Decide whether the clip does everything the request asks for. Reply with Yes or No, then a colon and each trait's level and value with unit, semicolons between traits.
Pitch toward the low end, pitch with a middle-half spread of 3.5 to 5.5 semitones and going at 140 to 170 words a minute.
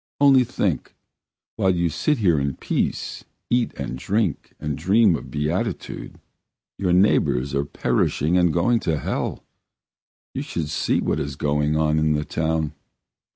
Yes: very low, 80 Hz; average, 4.4 semitones; average, 150 wpm